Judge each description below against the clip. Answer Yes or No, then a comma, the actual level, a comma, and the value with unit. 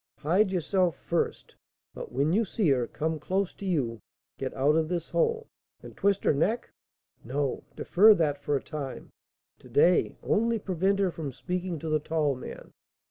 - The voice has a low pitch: No, medium, 165 Hz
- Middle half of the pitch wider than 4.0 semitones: Yes, average, 5.0 semitones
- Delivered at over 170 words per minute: Yes, average, 180 wpm